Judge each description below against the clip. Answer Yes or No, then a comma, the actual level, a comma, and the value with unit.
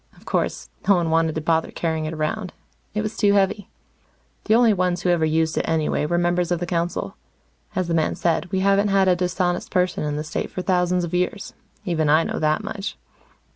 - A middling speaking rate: No, fast, 215 wpm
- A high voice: No, medium, 175 Hz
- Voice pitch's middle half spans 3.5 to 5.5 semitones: No, average, 2.8 semitones